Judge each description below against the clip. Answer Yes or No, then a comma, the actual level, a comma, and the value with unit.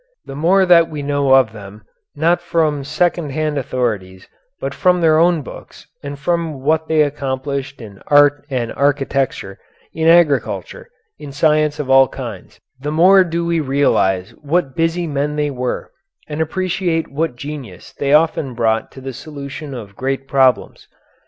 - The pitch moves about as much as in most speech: Yes, average, 3.4 semitones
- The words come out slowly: No, average, 160 wpm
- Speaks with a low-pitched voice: No, medium, 145 Hz